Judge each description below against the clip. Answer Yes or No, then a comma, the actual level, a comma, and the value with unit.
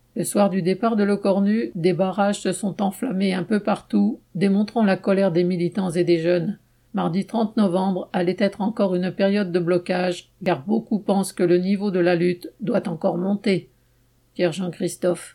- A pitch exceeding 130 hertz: Yes, high, 190 Hz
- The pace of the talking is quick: No, average, 185 wpm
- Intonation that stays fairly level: Yes, narrow, 2.1 semitones